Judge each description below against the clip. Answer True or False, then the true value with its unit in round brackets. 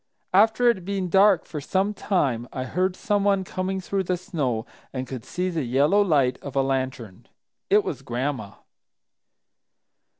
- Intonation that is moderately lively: False (6.9 semitones)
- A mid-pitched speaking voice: True (170 Hz)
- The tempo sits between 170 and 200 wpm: False (160 wpm)